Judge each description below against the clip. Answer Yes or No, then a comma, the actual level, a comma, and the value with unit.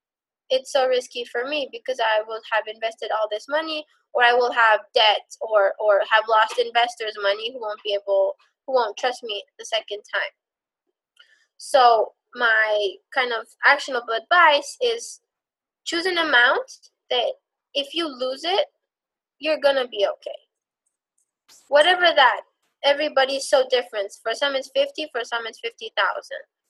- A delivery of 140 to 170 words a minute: Yes, average, 155 wpm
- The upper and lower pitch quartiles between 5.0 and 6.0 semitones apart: Yes, wide, 5.5 semitones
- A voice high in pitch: Yes, very high, 260 Hz